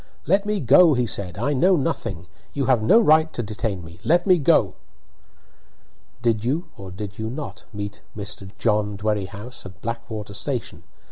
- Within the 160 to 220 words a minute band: Yes, average, 165 wpm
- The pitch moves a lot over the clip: Yes, wide, 6.0 semitones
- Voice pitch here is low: Yes, low, 115 Hz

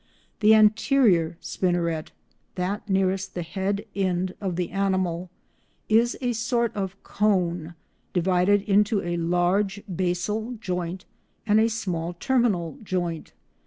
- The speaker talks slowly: Yes, slow, 120 wpm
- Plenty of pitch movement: No, average, 3.2 semitones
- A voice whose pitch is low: No, high, 190 Hz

